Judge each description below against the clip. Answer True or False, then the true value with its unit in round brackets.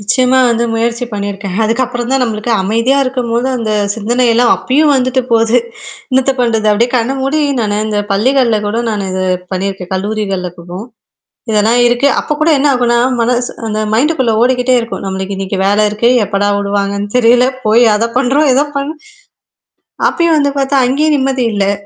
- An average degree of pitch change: True (3.8 semitones)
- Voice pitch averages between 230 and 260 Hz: True (235 Hz)